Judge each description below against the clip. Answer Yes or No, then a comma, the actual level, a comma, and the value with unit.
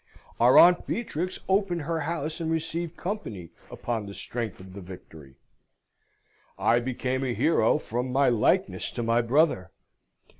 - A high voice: No, low, 130 Hz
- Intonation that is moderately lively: No, wide, 6.8 semitones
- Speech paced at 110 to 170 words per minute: Yes, average, 145 wpm